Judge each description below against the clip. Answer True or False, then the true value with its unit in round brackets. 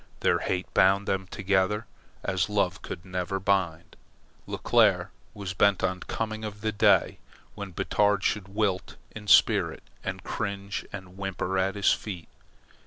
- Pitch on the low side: True (95 Hz)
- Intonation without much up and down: True (1.6 semitones)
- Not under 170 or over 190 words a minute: False (150 wpm)